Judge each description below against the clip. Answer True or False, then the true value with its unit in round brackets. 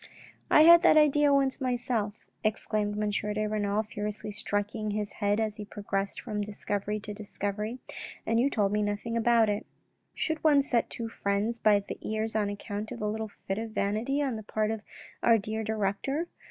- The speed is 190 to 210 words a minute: True (195 wpm)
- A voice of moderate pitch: False (215 Hz)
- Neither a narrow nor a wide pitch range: False (2.0 semitones)